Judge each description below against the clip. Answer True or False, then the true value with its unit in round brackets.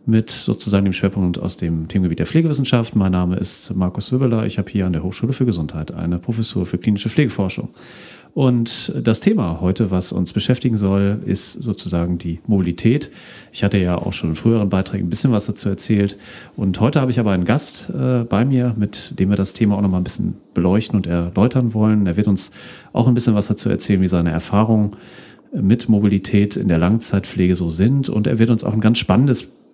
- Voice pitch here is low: True (100 Hz)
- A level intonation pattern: False (3.8 semitones)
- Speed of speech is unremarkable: False (205 wpm)